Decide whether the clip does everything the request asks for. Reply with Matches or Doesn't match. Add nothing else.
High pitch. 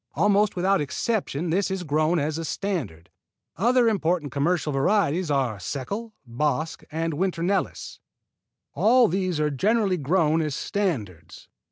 Doesn't match